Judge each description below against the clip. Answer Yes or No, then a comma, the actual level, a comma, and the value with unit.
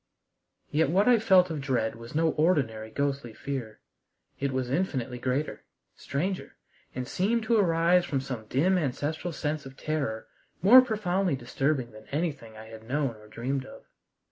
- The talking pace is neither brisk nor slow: Yes, average, 160 wpm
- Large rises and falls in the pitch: Yes, wide, 6.0 semitones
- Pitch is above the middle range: No, medium, 140 Hz